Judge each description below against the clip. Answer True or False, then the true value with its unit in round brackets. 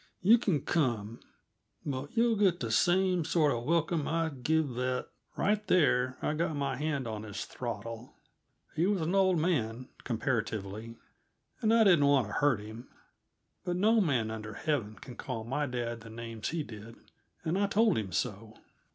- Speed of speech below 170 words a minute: False (175 wpm)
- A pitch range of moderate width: False (6.9 semitones)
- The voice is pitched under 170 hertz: True (135 Hz)